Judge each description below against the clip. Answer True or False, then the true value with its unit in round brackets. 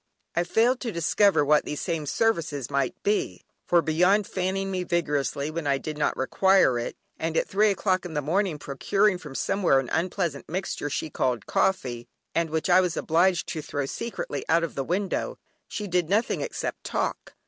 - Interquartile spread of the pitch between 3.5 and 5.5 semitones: True (4.6 semitones)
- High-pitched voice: False (170 Hz)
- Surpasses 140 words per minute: True (190 wpm)